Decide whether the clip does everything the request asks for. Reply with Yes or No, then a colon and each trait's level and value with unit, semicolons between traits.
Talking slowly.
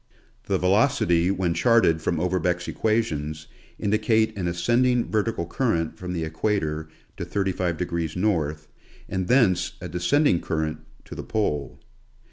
Yes: slow, 125 wpm